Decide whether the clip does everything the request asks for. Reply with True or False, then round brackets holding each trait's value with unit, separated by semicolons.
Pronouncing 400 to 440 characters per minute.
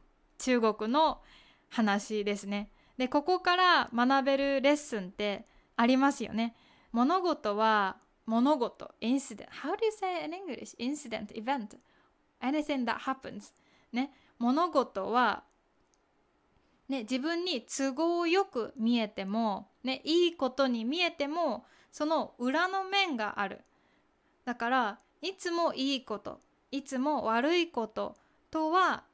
False (300 characters per minute)